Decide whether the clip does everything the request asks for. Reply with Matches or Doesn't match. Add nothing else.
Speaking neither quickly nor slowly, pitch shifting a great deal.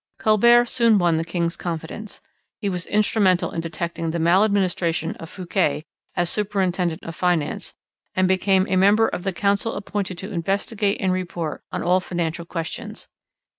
Doesn't match